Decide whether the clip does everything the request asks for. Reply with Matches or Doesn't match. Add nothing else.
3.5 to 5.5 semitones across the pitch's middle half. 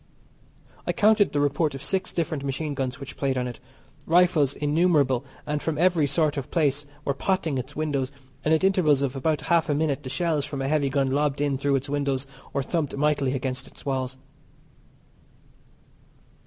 Doesn't match